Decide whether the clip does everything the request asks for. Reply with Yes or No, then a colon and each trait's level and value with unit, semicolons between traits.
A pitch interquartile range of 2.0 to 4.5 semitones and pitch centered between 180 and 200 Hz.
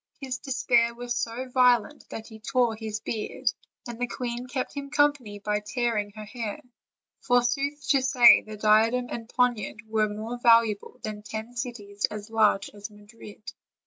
No: narrow, 2.5 semitones; high, 230 Hz